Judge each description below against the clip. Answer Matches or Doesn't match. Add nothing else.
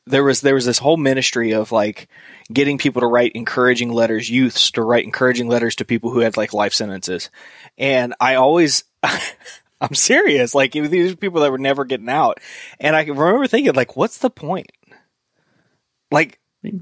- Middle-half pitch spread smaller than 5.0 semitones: Matches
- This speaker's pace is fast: Doesn't match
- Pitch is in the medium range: Doesn't match